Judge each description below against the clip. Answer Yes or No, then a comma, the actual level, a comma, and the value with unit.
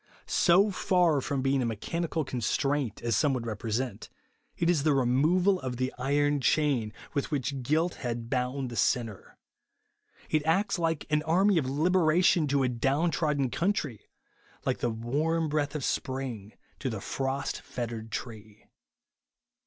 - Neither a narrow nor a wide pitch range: Yes, average, 4.7 semitones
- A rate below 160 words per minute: Yes, average, 150 wpm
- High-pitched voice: No, medium, 140 Hz